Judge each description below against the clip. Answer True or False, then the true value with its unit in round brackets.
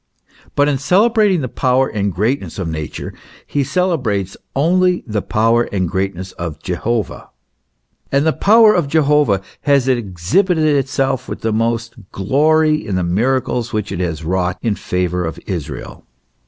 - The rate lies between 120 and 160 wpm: True (155 wpm)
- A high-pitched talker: False (120 Hz)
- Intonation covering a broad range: True (7.8 semitones)